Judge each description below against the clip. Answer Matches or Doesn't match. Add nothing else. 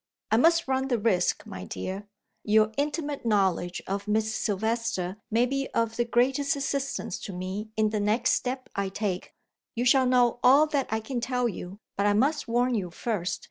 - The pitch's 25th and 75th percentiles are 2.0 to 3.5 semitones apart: Doesn't match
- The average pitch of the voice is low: Doesn't match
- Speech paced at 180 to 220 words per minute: Matches